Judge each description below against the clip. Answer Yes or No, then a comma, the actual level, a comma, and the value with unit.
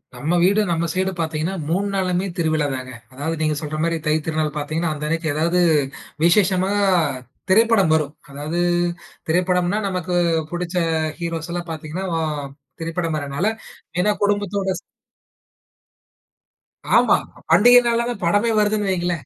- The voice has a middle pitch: Yes, medium, 175 Hz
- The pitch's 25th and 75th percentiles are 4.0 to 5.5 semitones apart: No, average, 3.4 semitones